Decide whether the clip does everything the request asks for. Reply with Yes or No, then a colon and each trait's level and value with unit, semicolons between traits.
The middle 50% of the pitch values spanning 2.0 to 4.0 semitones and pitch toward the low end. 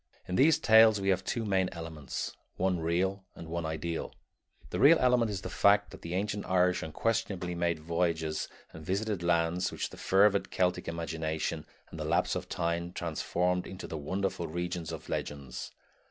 Yes: average, 2.9 semitones; very low, 90 Hz